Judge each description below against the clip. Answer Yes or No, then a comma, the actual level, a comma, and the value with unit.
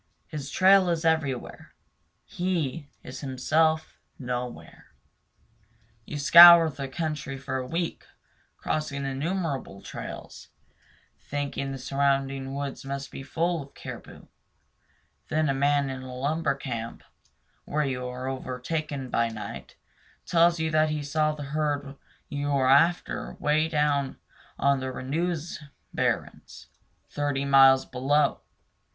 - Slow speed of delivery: Yes, slow, 120 wpm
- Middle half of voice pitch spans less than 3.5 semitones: Yes, average, 2.7 semitones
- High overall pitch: No, medium, 140 Hz